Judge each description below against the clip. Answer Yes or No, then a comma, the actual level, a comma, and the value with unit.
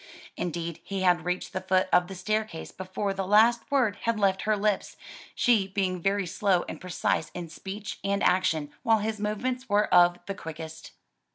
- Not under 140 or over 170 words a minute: No, average, 180 wpm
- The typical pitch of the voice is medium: No, high, 195 Hz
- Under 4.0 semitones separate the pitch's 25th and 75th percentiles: Yes, average, 2.9 semitones